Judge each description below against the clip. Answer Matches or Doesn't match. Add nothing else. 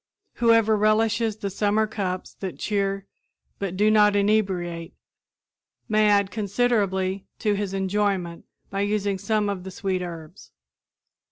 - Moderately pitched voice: Doesn't match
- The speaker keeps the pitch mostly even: Matches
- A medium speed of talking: Doesn't match